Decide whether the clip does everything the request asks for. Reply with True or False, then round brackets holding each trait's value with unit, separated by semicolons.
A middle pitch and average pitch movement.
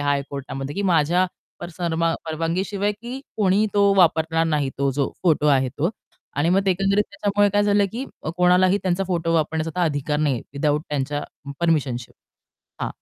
True (165 Hz; 4.9 semitones)